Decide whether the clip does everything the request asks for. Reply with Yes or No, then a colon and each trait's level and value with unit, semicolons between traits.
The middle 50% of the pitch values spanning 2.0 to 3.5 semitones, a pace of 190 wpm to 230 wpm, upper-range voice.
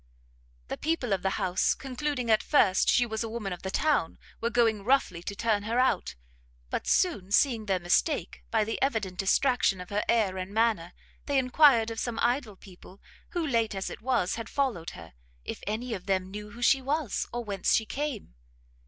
No: average, 4.6 semitones; average, 195 wpm; high, 225 Hz